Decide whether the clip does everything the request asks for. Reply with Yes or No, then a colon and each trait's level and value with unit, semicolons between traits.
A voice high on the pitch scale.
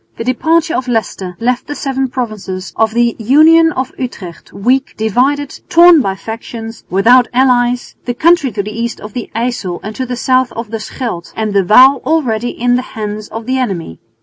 Yes: high, 240 Hz